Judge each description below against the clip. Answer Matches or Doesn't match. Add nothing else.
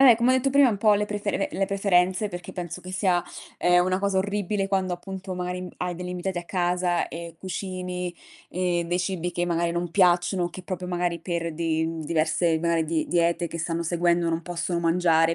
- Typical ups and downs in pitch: Doesn't match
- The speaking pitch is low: Doesn't match